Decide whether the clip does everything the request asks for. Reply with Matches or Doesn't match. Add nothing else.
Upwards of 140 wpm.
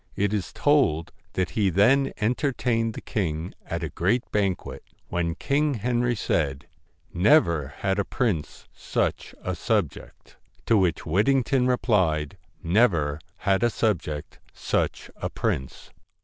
Doesn't match